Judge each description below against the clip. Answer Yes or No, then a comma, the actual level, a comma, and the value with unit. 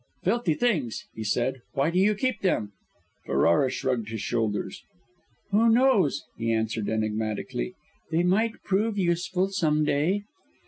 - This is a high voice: No, medium, 160 Hz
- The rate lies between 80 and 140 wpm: Yes, slow, 135 wpm